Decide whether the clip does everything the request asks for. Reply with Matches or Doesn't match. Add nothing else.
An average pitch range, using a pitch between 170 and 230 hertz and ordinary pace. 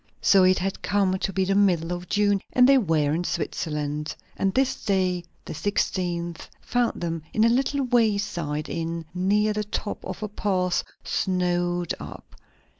Matches